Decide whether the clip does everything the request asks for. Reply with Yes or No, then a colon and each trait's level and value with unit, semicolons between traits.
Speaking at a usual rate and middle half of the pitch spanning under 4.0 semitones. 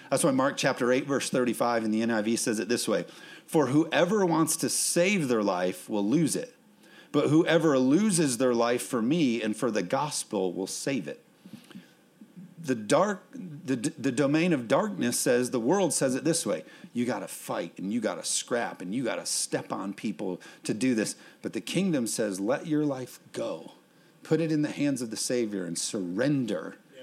No: average, 190 wpm; average, 5.3 semitones